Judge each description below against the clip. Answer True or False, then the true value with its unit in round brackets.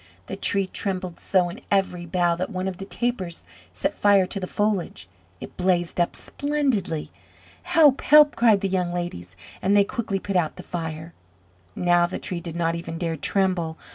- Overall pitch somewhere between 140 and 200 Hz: True (185 Hz)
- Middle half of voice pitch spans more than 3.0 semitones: False (2.6 semitones)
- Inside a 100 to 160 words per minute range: False (180 wpm)